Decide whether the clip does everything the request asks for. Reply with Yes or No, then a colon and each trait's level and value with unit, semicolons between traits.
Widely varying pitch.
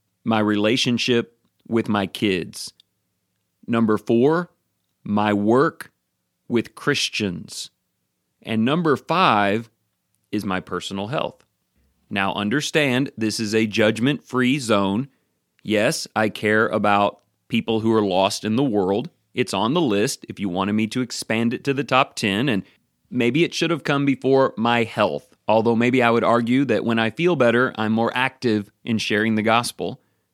No: average, 3.0 semitones